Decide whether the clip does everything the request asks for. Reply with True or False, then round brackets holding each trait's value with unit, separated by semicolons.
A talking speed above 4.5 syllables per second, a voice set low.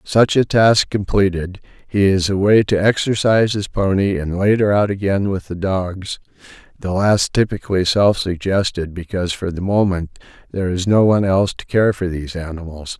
True (5.2 syllables/s; 95 Hz)